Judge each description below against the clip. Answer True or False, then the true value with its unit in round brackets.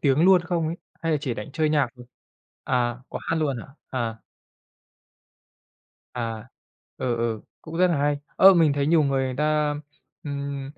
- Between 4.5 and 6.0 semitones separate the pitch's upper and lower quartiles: False (3.9 semitones)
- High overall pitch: False (140 Hz)